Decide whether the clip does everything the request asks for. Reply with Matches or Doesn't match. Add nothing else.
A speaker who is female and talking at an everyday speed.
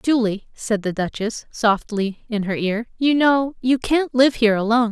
Matches